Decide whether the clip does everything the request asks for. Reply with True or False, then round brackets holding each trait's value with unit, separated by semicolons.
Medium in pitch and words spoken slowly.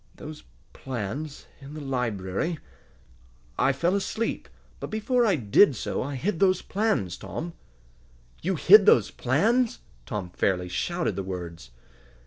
True (145 Hz; 130 wpm)